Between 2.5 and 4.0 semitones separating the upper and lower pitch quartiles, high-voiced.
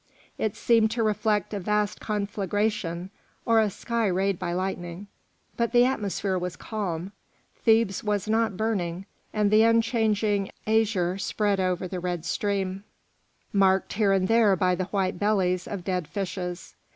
Yes: average, 2.8 semitones; high, 200 Hz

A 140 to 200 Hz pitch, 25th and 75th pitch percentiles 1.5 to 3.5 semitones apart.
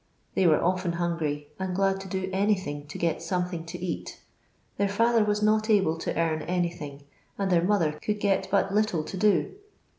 Yes: medium, 185 Hz; average, 3.2 semitones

